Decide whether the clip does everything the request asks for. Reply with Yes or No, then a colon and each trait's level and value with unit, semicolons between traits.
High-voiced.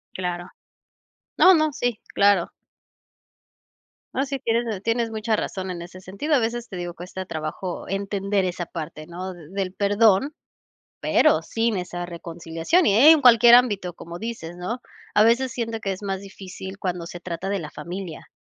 Yes: high, 195 Hz